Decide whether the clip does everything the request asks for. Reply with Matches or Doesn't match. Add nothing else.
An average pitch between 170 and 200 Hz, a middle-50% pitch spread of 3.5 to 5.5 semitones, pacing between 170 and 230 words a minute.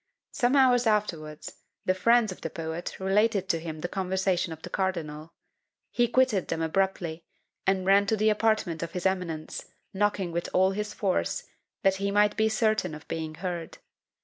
Matches